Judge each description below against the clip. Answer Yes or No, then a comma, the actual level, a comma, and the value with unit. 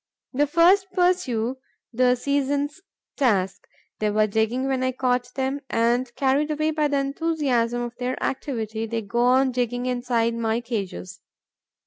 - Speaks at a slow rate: No, average, 145 wpm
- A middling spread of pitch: Yes, average, 3.3 semitones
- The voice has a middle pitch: No, very high, 250 Hz